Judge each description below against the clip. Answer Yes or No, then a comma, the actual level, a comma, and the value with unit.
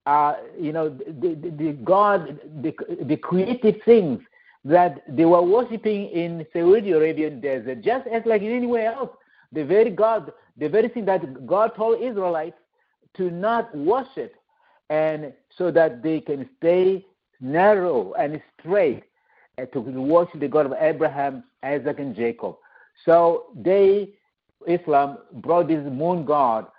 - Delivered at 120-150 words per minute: Yes, average, 145 wpm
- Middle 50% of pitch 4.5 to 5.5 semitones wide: Yes, average, 5.1 semitones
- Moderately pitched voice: Yes, medium, 170 Hz